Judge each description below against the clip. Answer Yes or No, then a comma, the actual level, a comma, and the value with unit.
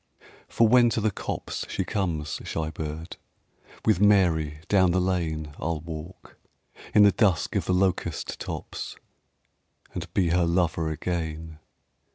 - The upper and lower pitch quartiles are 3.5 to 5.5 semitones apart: No, average, 3.1 semitones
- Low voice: Yes, very low, 85 Hz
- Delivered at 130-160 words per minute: Yes, average, 140 wpm